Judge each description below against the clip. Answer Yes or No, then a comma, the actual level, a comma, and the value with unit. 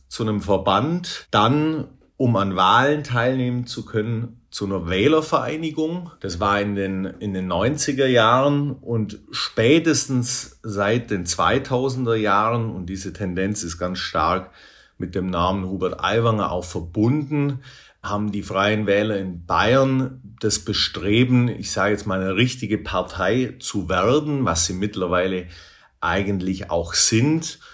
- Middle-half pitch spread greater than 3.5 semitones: Yes, average, 5.0 semitones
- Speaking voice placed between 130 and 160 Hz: No, low, 105 Hz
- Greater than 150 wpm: No, average, 135 wpm